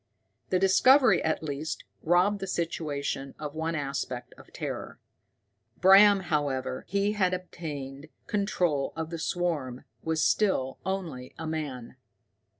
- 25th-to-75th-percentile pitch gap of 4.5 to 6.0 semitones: Yes, average, 4.9 semitones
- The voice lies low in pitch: No, medium, 160 Hz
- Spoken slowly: Yes, slow, 125 wpm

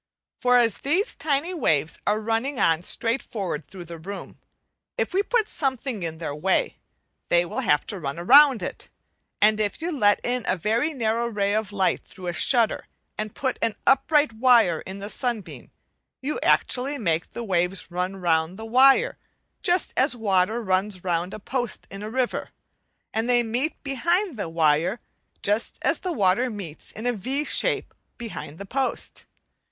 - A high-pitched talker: Yes, high, 220 Hz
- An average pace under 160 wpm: No, average, 175 wpm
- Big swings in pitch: Yes, wide, 5.9 semitones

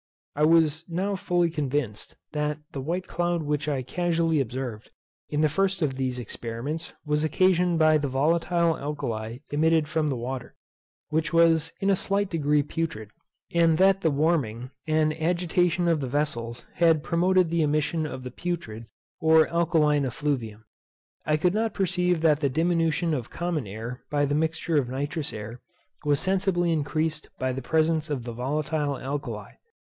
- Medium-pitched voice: Yes, medium, 155 Hz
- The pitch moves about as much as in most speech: Yes, average, 3.6 semitones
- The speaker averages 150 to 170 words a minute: Yes, average, 165 wpm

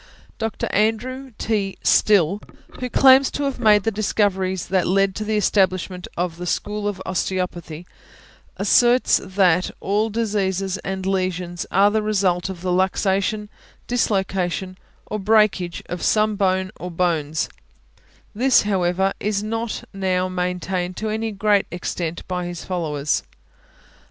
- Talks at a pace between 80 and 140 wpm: Yes, slow, 135 wpm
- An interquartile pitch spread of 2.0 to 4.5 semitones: Yes, average, 2.8 semitones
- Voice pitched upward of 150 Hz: Yes, high, 190 Hz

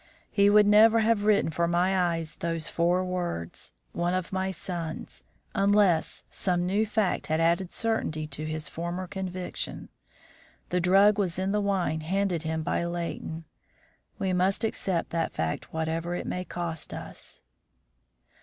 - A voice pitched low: No, medium, 180 Hz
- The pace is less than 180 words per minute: Yes, average, 150 wpm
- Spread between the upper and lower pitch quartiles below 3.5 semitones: Yes, average, 2.8 semitones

